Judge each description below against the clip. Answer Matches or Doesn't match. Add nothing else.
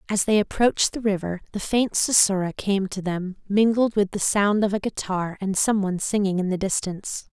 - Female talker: Matches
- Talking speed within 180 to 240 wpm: Matches